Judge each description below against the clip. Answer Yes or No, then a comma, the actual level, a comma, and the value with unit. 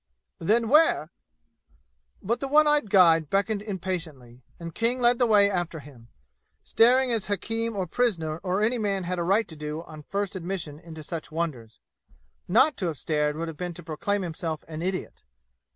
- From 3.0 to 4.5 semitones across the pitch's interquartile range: No, wide, 5.4 semitones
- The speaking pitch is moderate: Yes, medium, 180 Hz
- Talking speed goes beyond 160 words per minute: Yes, average, 180 wpm